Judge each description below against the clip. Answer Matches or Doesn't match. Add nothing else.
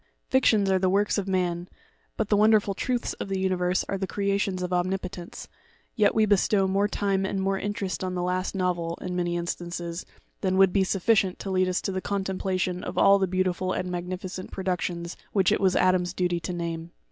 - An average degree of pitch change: Doesn't match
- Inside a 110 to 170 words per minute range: Doesn't match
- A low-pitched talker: Doesn't match